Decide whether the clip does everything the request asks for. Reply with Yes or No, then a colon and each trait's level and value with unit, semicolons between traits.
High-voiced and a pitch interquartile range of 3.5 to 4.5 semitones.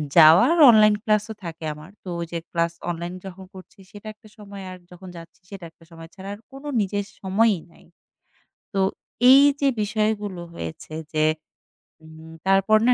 Yes: high, 195 Hz; average, 4.0 semitones